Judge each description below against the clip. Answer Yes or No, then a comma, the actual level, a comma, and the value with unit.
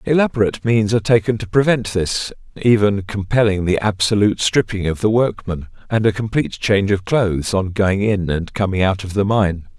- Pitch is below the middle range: Yes, low, 105 Hz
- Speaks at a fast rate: No, average, 185 wpm